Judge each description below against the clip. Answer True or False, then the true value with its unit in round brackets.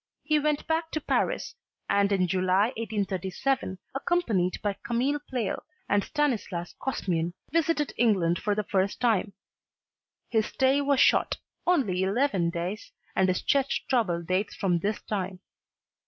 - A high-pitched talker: True (210 Hz)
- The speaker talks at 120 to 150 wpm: True (140 wpm)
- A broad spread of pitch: True (6.5 semitones)